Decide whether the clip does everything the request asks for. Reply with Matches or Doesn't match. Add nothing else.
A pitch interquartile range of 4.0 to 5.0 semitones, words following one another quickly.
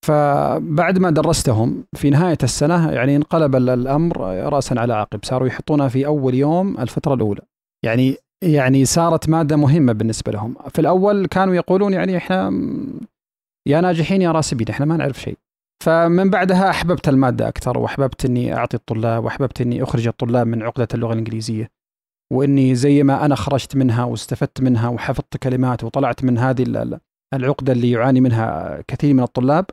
Matches